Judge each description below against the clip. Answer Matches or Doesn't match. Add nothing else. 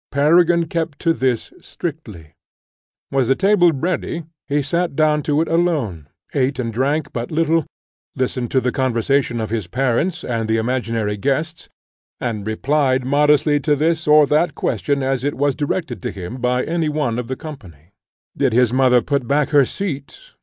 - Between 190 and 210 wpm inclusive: Doesn't match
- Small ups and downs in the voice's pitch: Doesn't match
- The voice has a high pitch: Doesn't match